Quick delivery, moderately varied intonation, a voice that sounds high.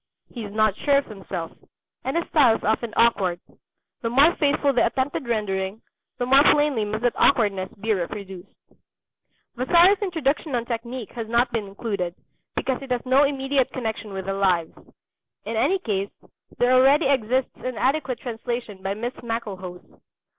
No: average, 160 wpm; average, 4.6 semitones; high, 235 Hz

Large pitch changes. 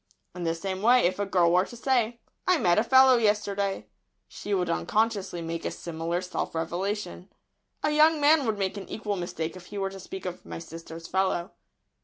No: average, 4.0 semitones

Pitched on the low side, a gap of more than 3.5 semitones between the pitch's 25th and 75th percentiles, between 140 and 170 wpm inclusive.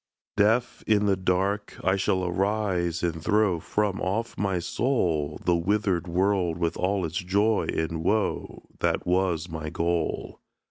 No: very low, 95 Hz; average, 3.2 semitones; average, 145 wpm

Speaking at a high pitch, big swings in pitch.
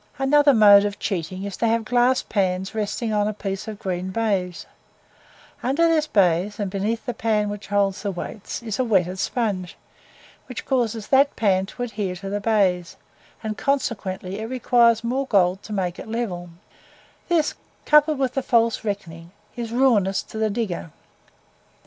No: high, 210 Hz; average, 3.8 semitones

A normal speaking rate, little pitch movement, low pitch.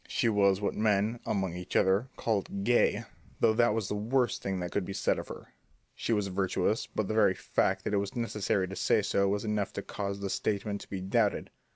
No: fast, 220 wpm; narrow, 2.1 semitones; low, 100 Hz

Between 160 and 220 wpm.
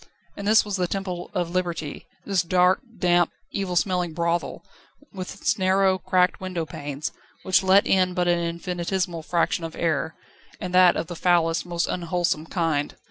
Yes: average, 165 wpm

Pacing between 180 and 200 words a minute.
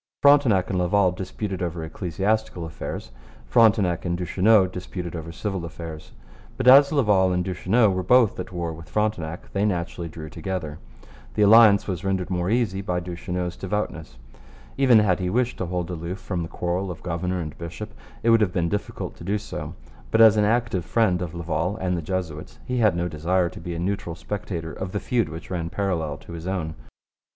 Yes: average, 195 wpm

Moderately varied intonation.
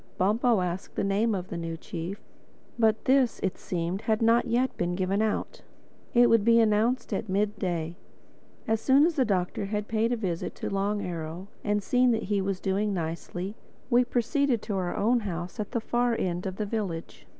Yes: average, 3.9 semitones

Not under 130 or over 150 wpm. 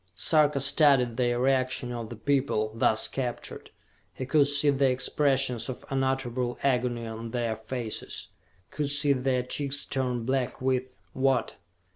Yes: average, 140 wpm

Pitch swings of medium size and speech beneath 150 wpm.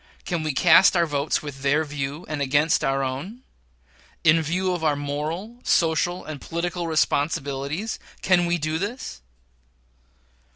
Yes: average, 3.4 semitones; average, 140 wpm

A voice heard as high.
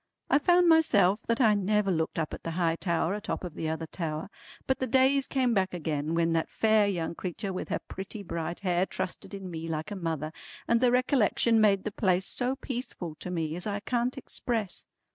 Yes: high, 195 Hz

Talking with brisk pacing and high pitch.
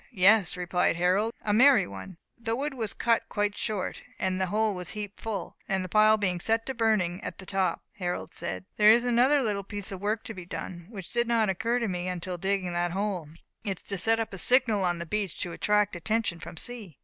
Yes: fast, 230 wpm; high, 200 Hz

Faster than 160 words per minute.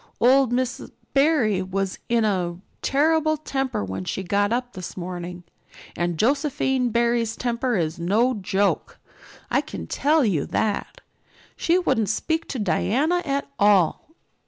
No: slow, 135 wpm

